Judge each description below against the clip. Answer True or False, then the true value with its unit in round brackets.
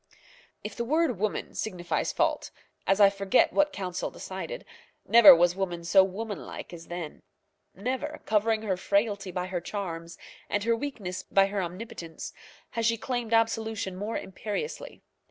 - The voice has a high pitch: True (200 Hz)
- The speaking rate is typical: True (150 wpm)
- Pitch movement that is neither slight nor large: True (3.8 semitones)